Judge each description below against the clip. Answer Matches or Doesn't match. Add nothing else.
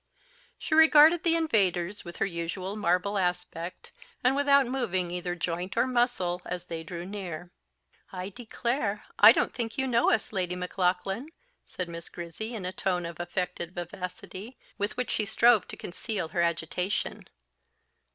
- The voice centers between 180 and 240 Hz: Matches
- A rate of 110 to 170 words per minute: Matches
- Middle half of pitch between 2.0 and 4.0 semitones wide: Doesn't match